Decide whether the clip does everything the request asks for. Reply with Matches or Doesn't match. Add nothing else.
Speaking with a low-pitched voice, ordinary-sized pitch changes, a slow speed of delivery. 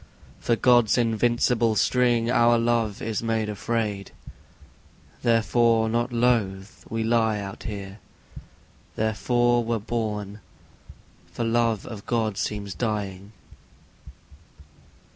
Doesn't match